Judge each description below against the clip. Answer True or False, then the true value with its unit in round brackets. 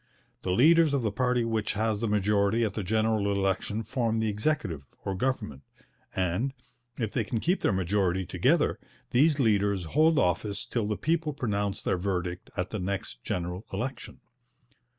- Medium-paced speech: True (165 wpm)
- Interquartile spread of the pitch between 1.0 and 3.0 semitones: False (4.0 semitones)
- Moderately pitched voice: False (105 Hz)